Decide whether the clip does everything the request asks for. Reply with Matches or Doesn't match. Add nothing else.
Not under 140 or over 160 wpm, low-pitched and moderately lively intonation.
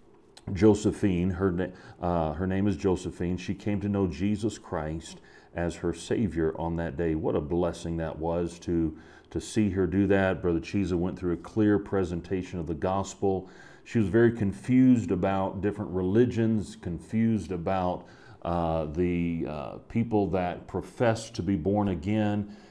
Matches